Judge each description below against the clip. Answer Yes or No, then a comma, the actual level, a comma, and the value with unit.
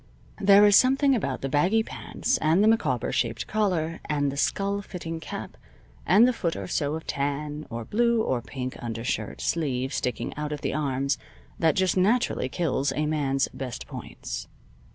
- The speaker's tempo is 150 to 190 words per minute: Yes, average, 175 wpm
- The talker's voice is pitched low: No, medium, 150 Hz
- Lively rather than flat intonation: Yes, wide, 6.6 semitones